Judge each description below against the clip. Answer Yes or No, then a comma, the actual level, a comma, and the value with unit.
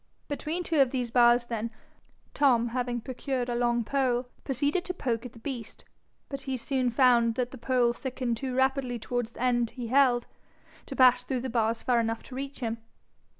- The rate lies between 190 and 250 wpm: Yes, average, 195 wpm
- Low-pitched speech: No, very high, 250 Hz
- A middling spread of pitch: No, narrow, 2.0 semitones